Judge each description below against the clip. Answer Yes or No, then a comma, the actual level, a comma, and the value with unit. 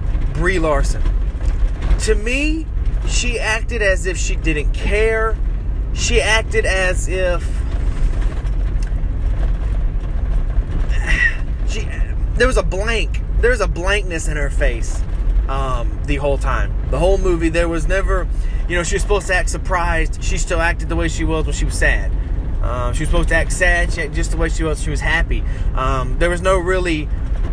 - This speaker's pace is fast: No, average, 170 wpm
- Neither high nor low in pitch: No, low, 130 Hz